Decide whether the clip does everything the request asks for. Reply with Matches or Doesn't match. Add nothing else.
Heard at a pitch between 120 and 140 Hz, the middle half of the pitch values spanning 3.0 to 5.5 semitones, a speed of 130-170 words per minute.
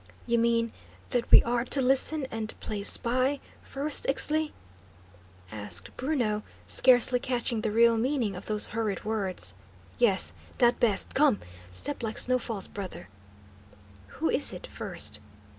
Doesn't match